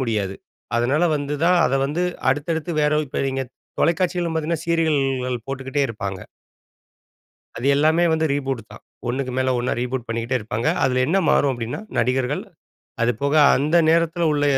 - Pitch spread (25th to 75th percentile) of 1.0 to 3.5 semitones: No, average, 4.3 semitones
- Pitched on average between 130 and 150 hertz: Yes, low, 135 Hz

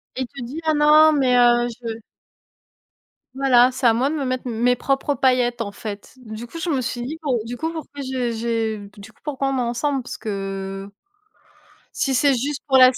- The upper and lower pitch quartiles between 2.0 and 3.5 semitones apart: Yes, average, 2.8 semitones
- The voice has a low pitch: No, very high, 250 Hz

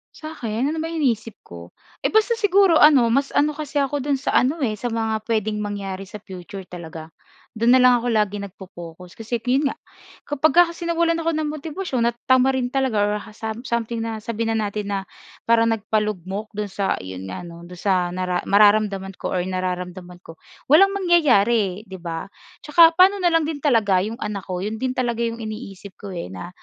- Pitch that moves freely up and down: Yes, wide, 6.2 semitones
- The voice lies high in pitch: Yes, high, 220 Hz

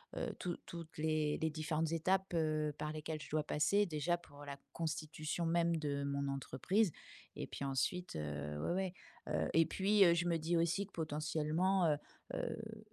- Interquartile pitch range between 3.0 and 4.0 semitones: No, narrow, 2.5 semitones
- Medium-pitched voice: Yes, medium, 160 Hz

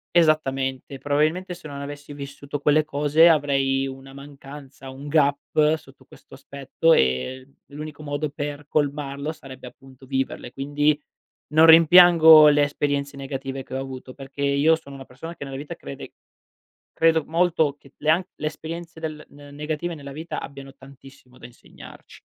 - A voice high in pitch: No, medium, 145 Hz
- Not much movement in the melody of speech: Yes, narrow, 2.2 semitones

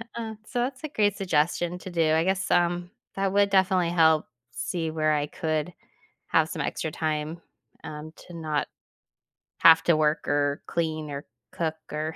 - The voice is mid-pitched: Yes, medium, 165 Hz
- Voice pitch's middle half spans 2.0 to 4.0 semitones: Yes, average, 2.9 semitones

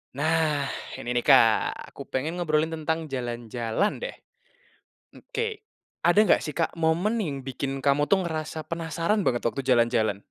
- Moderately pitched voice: Yes, medium, 155 Hz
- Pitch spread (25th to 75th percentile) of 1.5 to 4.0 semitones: No, average, 4.7 semitones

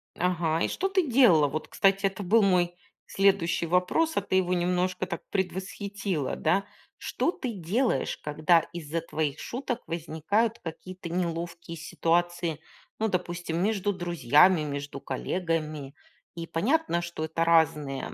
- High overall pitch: No, medium, 175 Hz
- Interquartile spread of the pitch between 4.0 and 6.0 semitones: No, average, 3.2 semitones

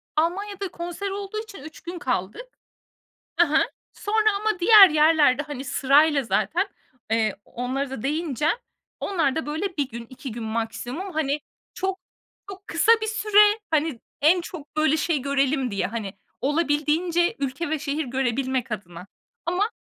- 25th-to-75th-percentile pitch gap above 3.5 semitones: Yes, wide, 5.5 semitones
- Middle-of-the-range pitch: No, very high, 300 Hz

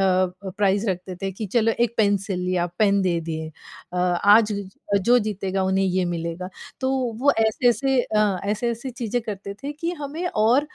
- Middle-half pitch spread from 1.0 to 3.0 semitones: No, average, 4.0 semitones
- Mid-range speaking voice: No, high, 200 Hz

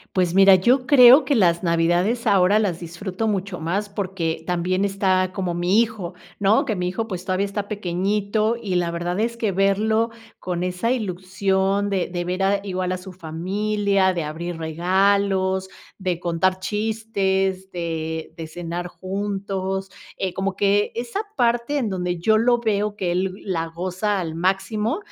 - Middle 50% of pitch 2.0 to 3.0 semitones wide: Yes, narrow, 2.5 semitones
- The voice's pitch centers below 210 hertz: Yes, high, 190 Hz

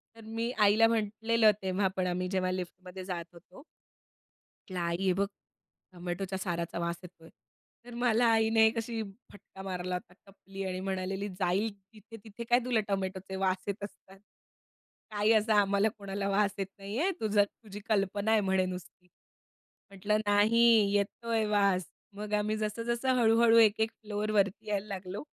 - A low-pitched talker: No, high, 200 Hz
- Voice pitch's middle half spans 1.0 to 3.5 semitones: Yes, average, 2.8 semitones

